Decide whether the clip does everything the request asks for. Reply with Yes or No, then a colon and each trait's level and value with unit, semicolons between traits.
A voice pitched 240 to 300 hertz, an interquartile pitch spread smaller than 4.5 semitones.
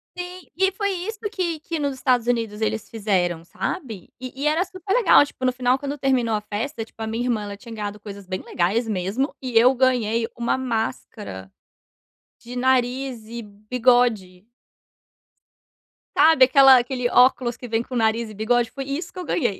Yes: high, 245 Hz; average, 3.6 semitones